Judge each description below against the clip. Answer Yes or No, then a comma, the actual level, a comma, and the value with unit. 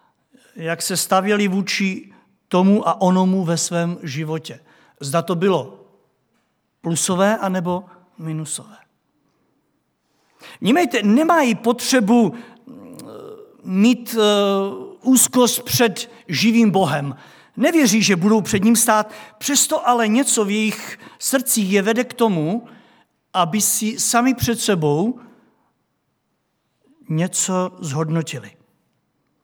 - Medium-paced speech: No, slow, 100 wpm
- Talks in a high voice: Yes, high, 210 Hz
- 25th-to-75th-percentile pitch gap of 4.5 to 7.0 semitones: Yes, average, 4.8 semitones